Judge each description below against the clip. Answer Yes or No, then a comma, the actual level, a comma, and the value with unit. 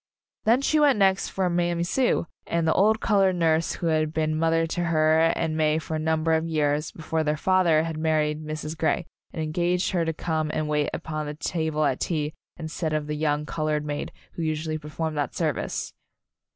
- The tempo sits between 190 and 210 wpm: Yes, average, 200 wpm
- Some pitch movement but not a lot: No, narrow, 1.7 semitones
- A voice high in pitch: No, medium, 160 Hz